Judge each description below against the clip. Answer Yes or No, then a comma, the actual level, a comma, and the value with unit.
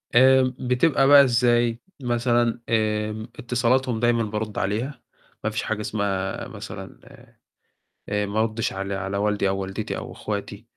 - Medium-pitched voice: No, low, 115 Hz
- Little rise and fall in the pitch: No, average, 3.0 semitones